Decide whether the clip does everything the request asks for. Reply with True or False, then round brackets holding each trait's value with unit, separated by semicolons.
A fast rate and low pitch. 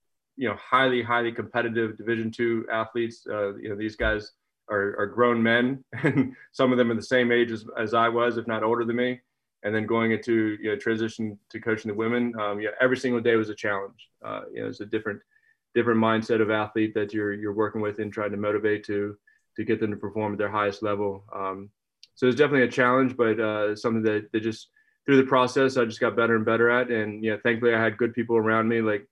True (240 wpm; 115 Hz)